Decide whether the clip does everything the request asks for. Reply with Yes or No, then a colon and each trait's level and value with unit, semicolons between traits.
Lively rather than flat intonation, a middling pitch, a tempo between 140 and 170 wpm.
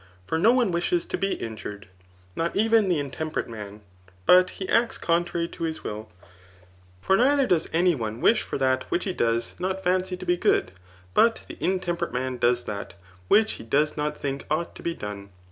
No: wide, 7.5 semitones; medium, 165 Hz; average, 195 wpm